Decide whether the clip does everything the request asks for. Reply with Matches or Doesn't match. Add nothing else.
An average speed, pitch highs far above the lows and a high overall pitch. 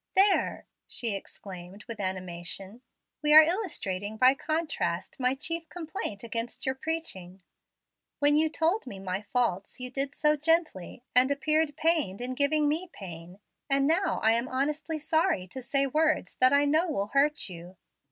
Matches